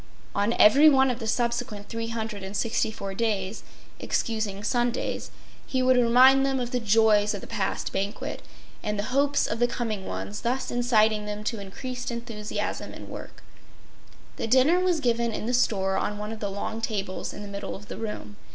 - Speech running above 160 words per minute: Yes, average, 180 wpm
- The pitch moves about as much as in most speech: Yes, average, 3.0 semitones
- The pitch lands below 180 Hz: No, high, 225 Hz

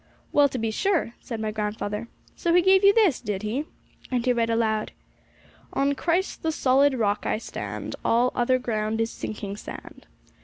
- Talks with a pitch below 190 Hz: No, high, 235 Hz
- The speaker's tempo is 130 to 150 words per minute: No, average, 180 wpm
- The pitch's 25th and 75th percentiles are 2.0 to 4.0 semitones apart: No, average, 4.8 semitones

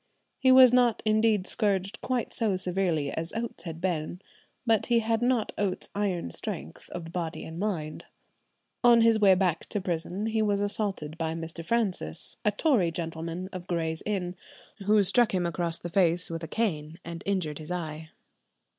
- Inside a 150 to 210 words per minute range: Yes, average, 170 wpm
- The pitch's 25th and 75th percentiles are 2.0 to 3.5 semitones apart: No, average, 4.6 semitones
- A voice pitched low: No, medium, 185 Hz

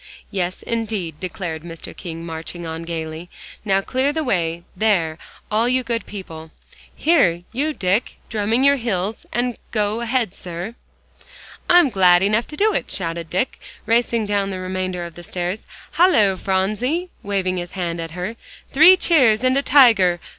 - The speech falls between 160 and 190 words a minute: No, average, 150 wpm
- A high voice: Yes, high, 195 Hz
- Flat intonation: No, average, 5.2 semitones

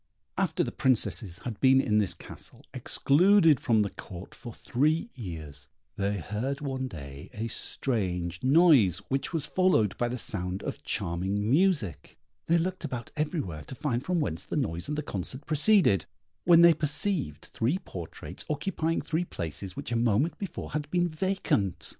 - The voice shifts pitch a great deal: Yes, wide, 8.2 semitones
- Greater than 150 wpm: Yes, average, 165 wpm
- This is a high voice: No, low, 130 Hz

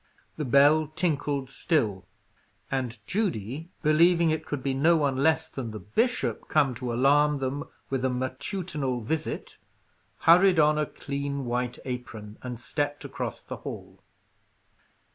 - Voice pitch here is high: No, medium, 140 Hz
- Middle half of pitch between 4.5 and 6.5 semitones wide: No, average, 3.8 semitones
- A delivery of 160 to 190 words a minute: No, average, 140 wpm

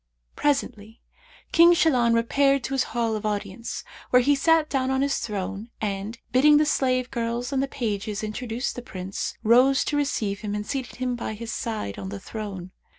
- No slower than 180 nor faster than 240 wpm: Yes, average, 185 wpm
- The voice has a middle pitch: No, high, 235 Hz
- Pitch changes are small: No, average, 4.3 semitones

